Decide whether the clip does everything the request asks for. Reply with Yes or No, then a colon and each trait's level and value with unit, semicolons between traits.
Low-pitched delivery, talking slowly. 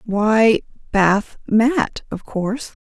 No: high, 220 Hz; slow, 85 wpm